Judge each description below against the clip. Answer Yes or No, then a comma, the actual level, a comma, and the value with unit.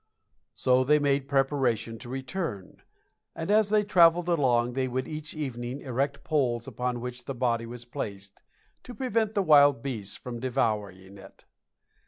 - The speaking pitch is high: No, low, 130 Hz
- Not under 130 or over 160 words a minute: Yes, average, 155 wpm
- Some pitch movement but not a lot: Yes, average, 4.1 semitones